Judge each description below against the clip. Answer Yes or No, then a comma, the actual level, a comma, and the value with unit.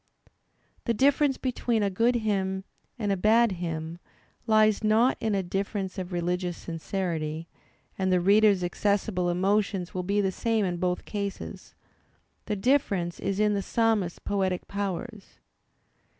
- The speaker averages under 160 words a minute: Yes, average, 140 wpm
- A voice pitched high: Yes, high, 195 Hz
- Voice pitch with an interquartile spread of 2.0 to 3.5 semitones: Yes, average, 3.2 semitones